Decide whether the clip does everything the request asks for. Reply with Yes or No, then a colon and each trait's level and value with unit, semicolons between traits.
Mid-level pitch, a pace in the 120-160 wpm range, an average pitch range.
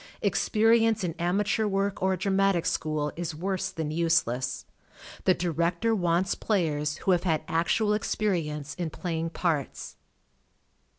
Yes: medium, 175 Hz; slow, 135 wpm; average, 3.4 semitones